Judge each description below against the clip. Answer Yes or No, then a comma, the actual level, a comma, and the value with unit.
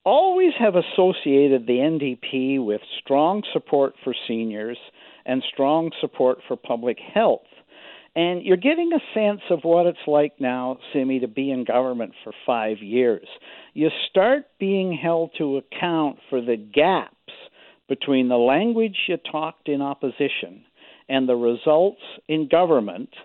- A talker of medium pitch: Yes, medium, 145 Hz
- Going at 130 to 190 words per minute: Yes, average, 140 wpm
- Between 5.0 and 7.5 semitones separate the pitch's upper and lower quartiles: Yes, wide, 5.4 semitones